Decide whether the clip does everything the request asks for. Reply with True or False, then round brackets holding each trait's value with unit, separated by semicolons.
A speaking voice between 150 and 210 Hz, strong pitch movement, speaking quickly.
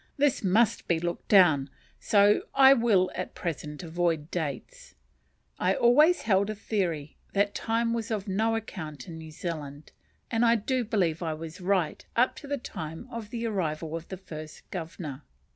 False (190 Hz; 5.9 semitones; 170 wpm)